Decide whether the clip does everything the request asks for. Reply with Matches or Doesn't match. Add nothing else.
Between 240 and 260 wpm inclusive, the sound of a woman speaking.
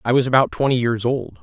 Doesn't match